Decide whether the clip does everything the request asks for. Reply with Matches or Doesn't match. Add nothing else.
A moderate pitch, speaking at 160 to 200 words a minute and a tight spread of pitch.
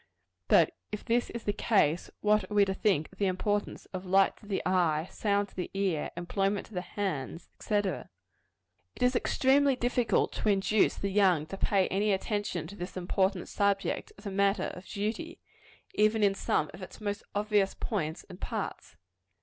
Doesn't match